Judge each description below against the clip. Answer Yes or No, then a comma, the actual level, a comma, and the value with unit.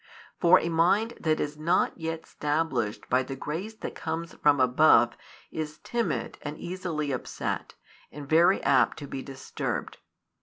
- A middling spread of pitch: Yes, average, 3.4 semitones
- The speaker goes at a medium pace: Yes, average, 150 wpm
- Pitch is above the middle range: No, medium, 155 Hz